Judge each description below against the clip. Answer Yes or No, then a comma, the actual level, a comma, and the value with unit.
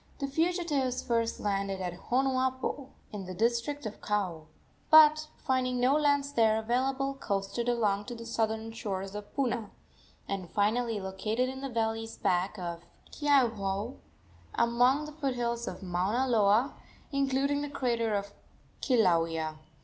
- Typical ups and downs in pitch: Yes, average, 4.7 semitones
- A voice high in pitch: Yes, high, 235 Hz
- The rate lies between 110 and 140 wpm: Yes, slow, 135 wpm